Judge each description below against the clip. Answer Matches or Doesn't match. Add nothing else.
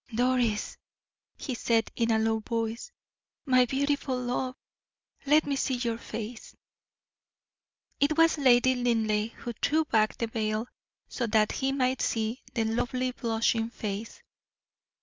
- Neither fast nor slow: Doesn't match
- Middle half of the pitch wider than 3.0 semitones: Doesn't match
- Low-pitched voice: Doesn't match